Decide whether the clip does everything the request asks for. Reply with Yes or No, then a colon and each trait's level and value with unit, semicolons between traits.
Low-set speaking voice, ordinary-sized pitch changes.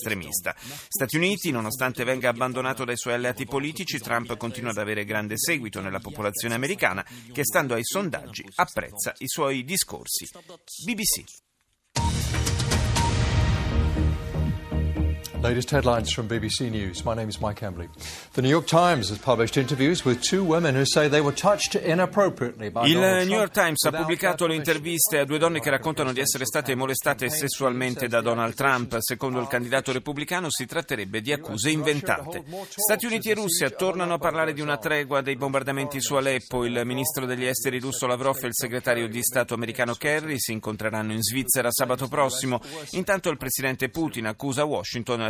Yes: low, 130 Hz; average, 4.6 semitones